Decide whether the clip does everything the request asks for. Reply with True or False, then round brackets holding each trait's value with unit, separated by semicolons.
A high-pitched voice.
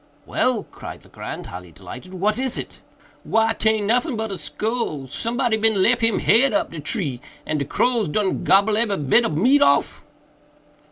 True (220 Hz)